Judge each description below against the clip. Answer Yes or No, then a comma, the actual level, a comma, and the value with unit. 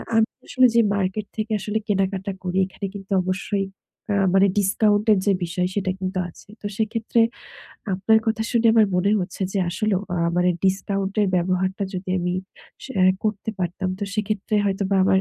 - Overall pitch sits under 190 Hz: No, high, 195 Hz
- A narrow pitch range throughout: Yes, narrow, 2.3 semitones